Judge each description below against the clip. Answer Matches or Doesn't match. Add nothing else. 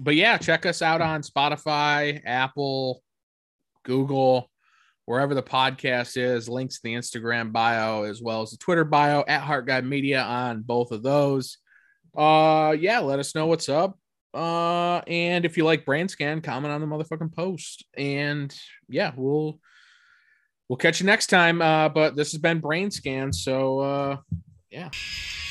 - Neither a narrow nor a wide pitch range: Matches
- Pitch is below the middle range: Doesn't match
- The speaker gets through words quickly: Doesn't match